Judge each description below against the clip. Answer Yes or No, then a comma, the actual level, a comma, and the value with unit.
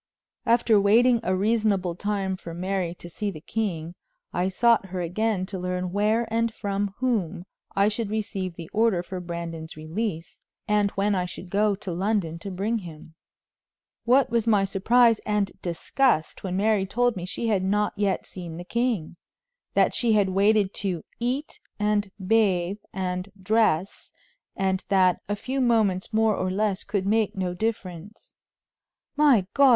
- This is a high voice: Yes, high, 200 Hz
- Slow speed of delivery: No, average, 160 wpm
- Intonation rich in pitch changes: No, average, 3.2 semitones